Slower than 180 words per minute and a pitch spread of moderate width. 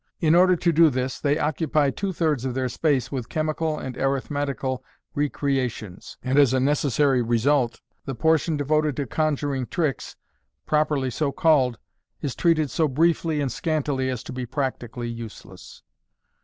Yes: average, 155 wpm; average, 3.1 semitones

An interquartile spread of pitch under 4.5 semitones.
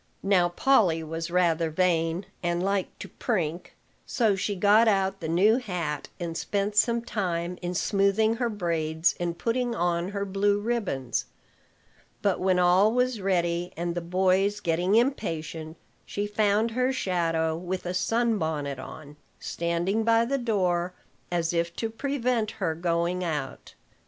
Yes: average, 3.8 semitones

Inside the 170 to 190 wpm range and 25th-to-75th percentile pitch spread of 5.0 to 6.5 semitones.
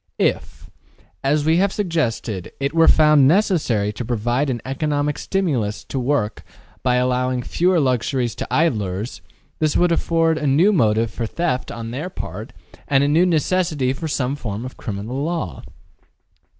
No: average, 155 wpm; wide, 5.4 semitones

